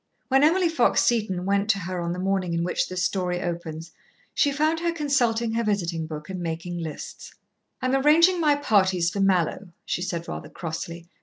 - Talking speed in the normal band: Yes, average, 185 wpm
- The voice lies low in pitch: No, high, 190 Hz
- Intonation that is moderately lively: No, wide, 7.0 semitones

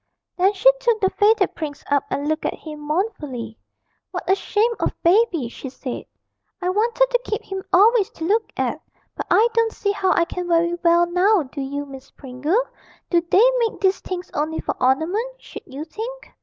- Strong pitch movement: Yes, wide, 6.2 semitones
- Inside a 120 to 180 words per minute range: No, average, 195 wpm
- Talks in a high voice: Yes, very high, 360 Hz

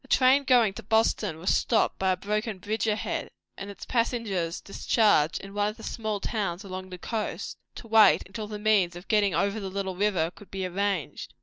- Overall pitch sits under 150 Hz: No, high, 205 Hz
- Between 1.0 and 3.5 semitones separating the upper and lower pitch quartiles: Yes, average, 2.7 semitones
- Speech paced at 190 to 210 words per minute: Yes, fast, 205 wpm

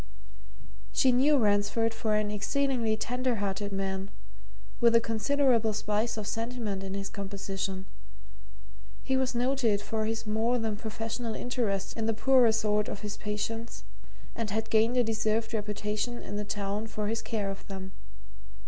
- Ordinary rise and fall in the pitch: No, narrow, 2.1 semitones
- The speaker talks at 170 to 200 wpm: No, average, 155 wpm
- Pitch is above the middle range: Yes, high, 220 Hz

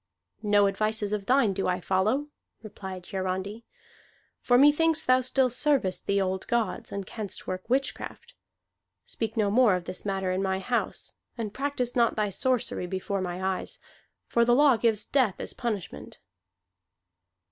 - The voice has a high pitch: Yes, high, 215 Hz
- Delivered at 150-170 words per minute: Yes, average, 155 wpm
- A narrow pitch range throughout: No, average, 4.7 semitones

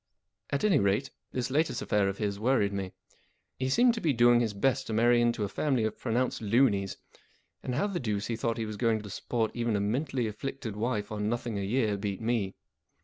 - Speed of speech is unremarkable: No, fast, 215 wpm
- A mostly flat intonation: No, average, 3.7 semitones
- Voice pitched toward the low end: Yes, low, 115 Hz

